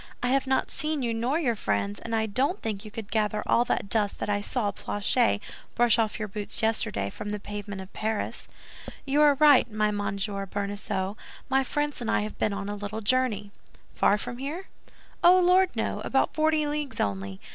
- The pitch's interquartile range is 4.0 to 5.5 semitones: Yes, average, 4.7 semitones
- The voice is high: Yes, high, 220 Hz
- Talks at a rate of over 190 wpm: Yes, average, 200 wpm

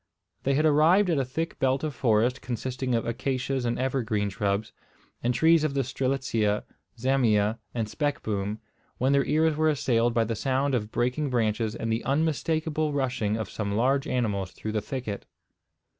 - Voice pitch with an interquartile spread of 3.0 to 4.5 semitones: Yes, average, 4.0 semitones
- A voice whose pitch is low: Yes, low, 125 Hz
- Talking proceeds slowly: No, average, 170 wpm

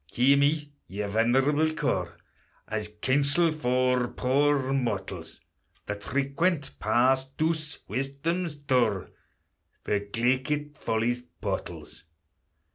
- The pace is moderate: No, slow, 95 wpm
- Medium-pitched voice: No, low, 130 Hz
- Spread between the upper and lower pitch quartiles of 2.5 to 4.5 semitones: Yes, average, 3.9 semitones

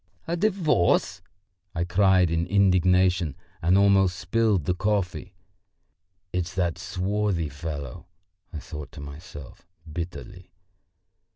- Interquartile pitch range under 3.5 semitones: Yes, average, 2.8 semitones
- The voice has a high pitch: No, very low, 90 Hz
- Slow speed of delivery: Yes, slow, 105 wpm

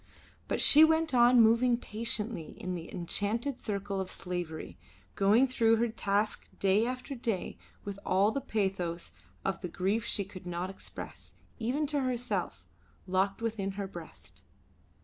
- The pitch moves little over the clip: No, average, 3.9 semitones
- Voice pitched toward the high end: Yes, high, 210 Hz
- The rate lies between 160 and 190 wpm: No, average, 150 wpm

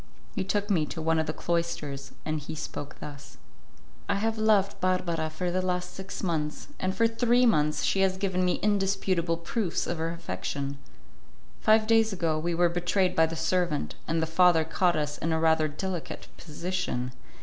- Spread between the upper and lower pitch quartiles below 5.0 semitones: Yes, average, 3.3 semitones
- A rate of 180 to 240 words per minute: Yes, average, 185 wpm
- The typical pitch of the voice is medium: Yes, medium, 170 Hz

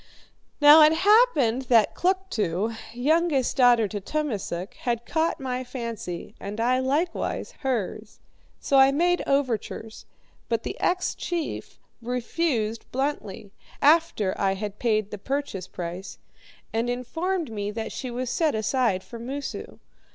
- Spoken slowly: Yes, slow, 130 wpm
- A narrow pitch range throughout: No, wide, 5.4 semitones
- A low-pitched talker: No, high, 245 Hz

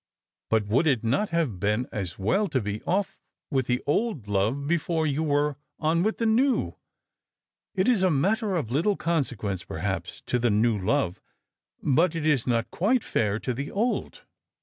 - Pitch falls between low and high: Yes, medium, 145 Hz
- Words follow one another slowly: No, average, 175 wpm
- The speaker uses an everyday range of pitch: No, wide, 8.1 semitones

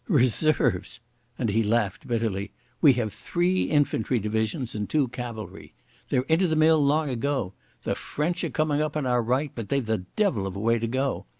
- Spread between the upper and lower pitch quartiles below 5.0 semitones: No, wide, 5.4 semitones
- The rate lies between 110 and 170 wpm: No, average, 190 wpm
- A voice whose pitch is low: Yes, low, 125 Hz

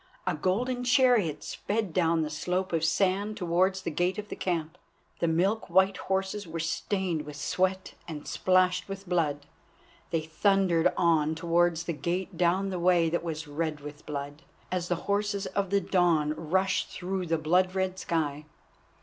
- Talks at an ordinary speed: Yes, average, 165 wpm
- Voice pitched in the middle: Yes, medium, 175 Hz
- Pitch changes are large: No, average, 2.9 semitones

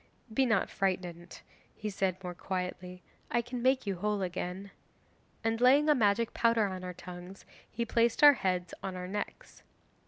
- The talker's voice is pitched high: Yes, high, 195 Hz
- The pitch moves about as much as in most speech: Yes, average, 4.2 semitones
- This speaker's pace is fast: No, average, 165 wpm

